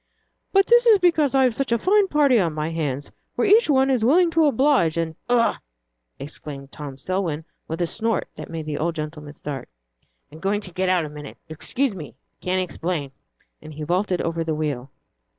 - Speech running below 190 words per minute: No, average, 200 wpm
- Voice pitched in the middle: Yes, medium, 175 Hz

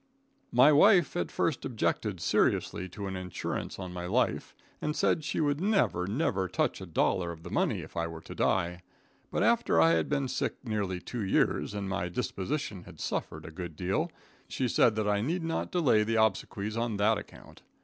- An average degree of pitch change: No, wide, 6.8 semitones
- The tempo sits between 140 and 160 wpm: No, average, 195 wpm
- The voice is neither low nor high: No, low, 105 Hz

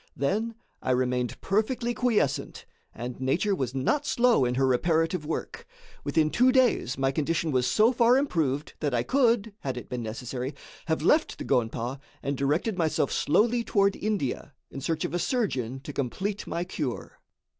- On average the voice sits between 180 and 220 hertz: No, medium, 155 Hz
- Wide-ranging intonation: Yes, wide, 8.5 semitones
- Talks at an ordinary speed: Yes, average, 165 wpm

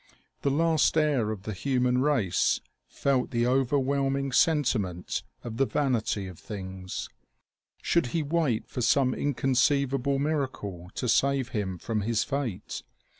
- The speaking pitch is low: Yes, low, 130 Hz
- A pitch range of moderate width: Yes, average, 4.3 semitones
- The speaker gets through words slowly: Yes, slow, 130 wpm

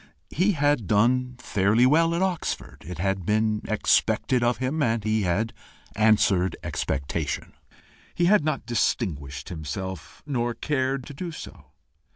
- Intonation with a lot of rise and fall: Yes, wide, 6.5 semitones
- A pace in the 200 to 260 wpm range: No, average, 140 wpm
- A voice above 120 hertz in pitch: No, low, 115 Hz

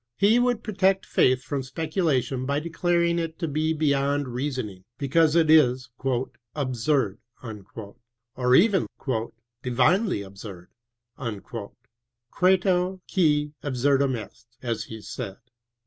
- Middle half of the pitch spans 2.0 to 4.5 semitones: No, wide, 5.4 semitones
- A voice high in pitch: No, medium, 140 Hz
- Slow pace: Yes, slow, 115 wpm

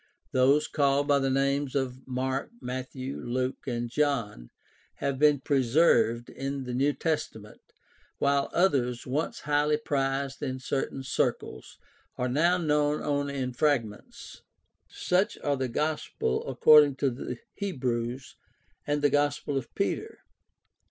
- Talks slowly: Yes, slow, 130 wpm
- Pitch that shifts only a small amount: Yes, narrow, 2.3 semitones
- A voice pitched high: No, low, 135 Hz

